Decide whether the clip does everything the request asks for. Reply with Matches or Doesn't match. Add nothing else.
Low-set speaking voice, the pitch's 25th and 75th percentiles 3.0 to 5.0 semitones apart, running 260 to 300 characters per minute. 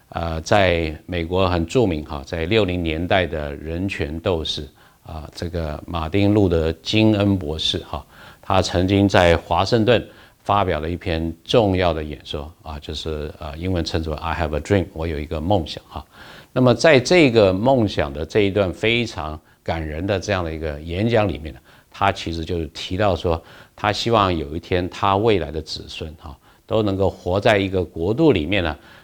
Doesn't match